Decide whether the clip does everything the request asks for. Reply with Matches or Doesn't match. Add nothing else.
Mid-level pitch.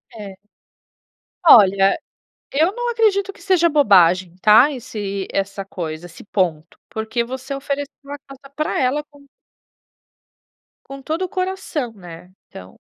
Doesn't match